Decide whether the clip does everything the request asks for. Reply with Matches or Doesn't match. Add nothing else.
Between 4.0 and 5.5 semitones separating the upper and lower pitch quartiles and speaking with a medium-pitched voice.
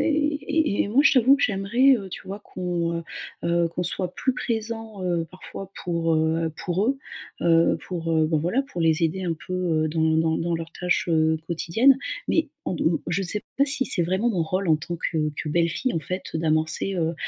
Matches